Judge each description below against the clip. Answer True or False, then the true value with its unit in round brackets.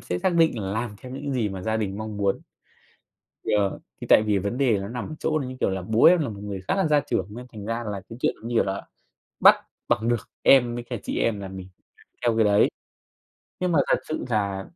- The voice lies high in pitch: False (110 Hz)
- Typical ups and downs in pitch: True (3.9 semitones)